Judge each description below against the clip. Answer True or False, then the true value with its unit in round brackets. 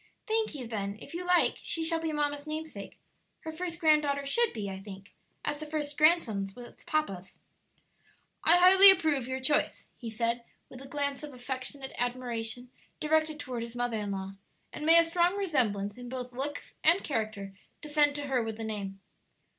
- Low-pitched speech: False (275 Hz)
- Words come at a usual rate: True (180 wpm)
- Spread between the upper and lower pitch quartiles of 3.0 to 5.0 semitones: False (5.5 semitones)